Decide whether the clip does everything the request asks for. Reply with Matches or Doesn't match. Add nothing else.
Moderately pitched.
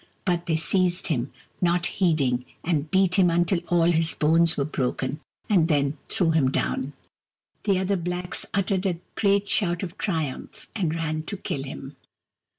Matches